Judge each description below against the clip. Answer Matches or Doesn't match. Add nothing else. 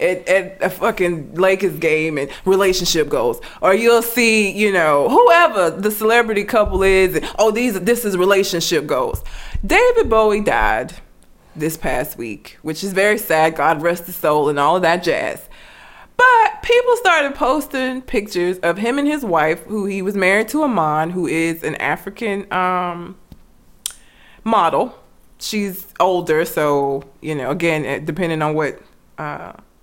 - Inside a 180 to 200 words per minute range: Doesn't match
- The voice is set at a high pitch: Matches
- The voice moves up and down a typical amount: Doesn't match